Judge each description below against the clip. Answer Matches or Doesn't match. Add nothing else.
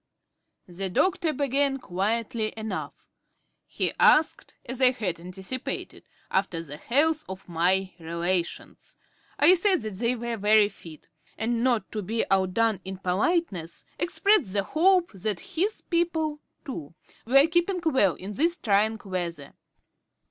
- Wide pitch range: Matches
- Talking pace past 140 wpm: Doesn't match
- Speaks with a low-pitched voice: Doesn't match